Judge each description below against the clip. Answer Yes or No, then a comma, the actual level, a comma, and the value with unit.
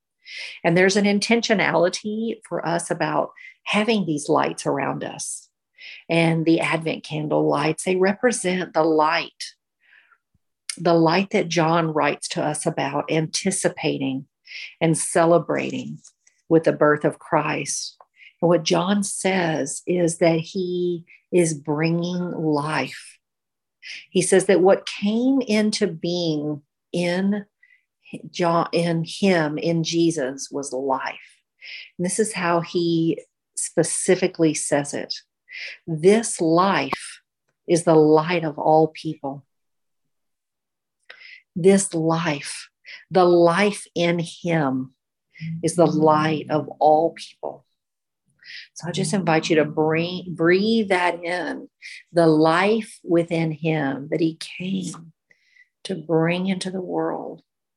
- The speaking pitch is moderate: Yes, medium, 170 Hz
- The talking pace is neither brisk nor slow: No, slow, 115 wpm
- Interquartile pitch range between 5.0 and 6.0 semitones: No, average, 3.3 semitones